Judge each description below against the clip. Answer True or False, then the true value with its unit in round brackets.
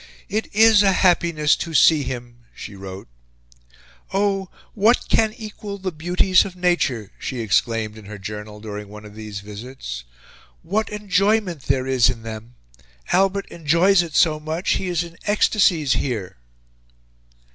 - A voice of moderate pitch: True (160 Hz)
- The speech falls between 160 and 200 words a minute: False (145 wpm)